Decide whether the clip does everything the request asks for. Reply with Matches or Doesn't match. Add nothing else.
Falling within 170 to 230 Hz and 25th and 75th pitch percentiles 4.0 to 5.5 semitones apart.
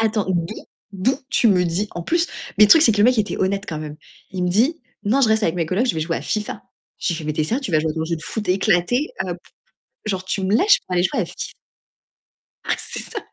Matches